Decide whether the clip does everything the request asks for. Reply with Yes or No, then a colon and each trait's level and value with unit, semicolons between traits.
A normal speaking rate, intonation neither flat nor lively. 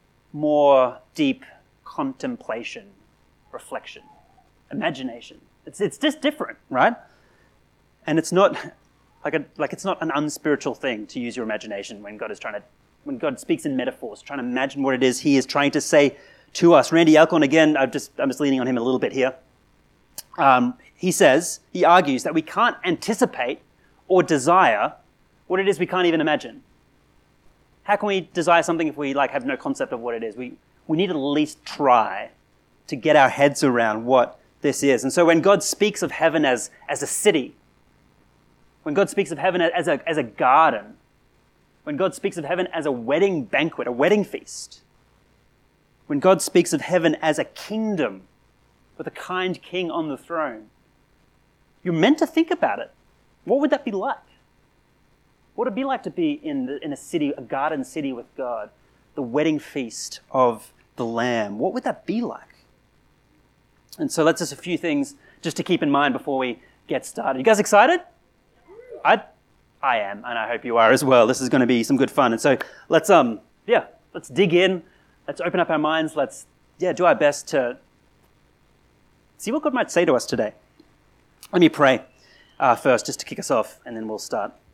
No: average, 195 wpm; wide, 6.8 semitones